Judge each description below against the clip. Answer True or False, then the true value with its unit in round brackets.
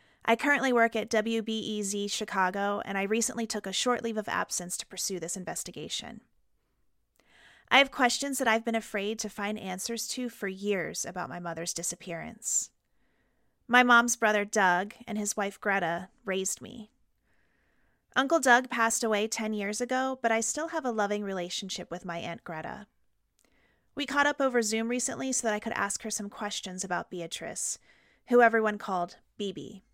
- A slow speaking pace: False (170 wpm)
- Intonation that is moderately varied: True (3.3 semitones)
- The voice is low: False (215 Hz)